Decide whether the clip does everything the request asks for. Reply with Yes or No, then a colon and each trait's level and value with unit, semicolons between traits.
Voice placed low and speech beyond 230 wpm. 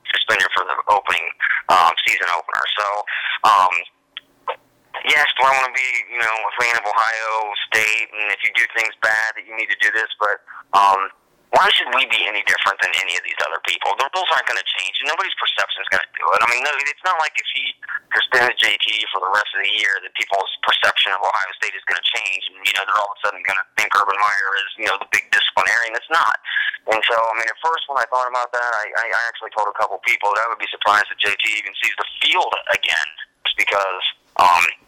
Yes: low, 115 Hz; fast, 240 wpm